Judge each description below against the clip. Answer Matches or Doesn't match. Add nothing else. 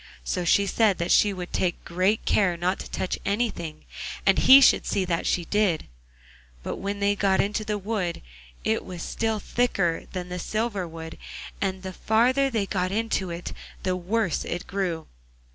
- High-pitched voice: Matches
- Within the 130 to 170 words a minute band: Doesn't match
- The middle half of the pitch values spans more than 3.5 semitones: Doesn't match